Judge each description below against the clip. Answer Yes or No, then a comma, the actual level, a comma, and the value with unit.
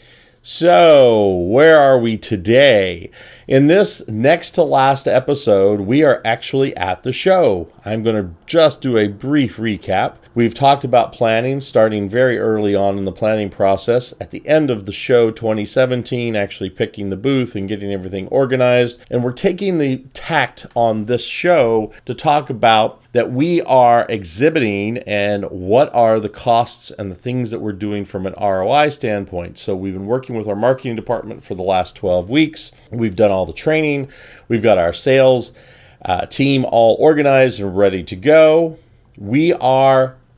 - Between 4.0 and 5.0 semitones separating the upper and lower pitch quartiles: Yes, average, 4.4 semitones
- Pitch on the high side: No, low, 120 Hz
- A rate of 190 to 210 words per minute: No, average, 170 wpm